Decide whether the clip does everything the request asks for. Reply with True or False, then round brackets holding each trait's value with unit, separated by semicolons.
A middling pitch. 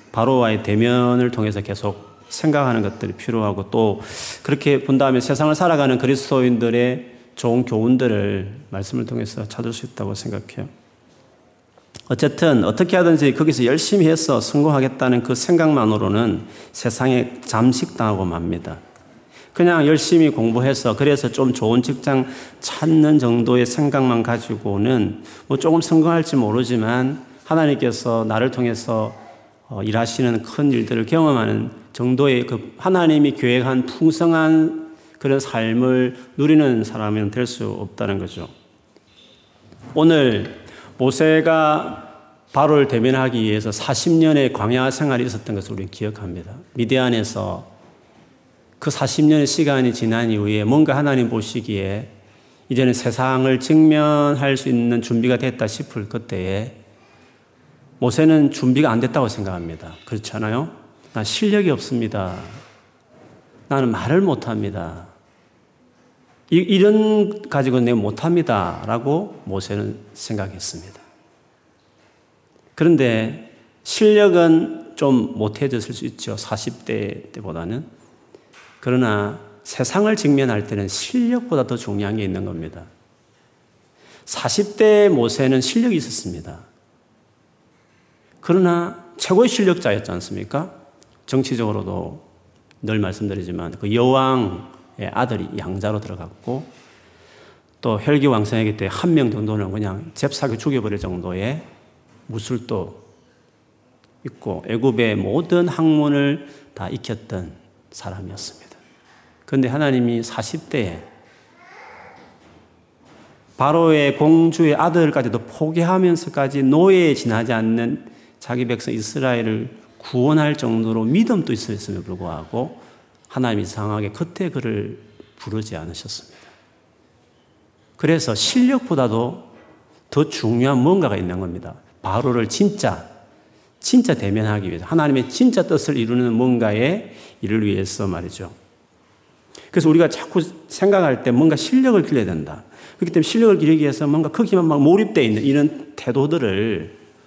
False (125 Hz)